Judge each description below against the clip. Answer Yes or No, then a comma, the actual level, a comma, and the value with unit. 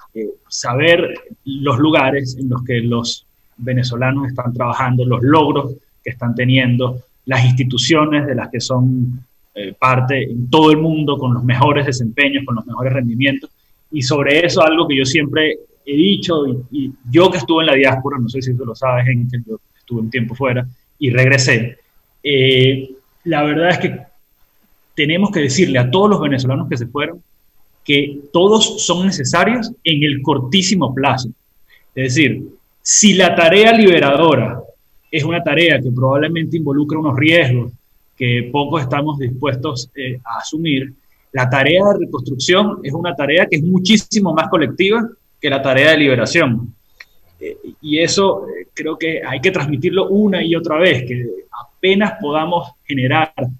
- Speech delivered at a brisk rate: No, average, 165 wpm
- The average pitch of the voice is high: No, medium, 140 Hz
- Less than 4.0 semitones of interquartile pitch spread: No, average, 4.6 semitones